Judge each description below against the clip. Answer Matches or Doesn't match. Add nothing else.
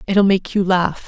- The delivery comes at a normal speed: Doesn't match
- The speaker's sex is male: Doesn't match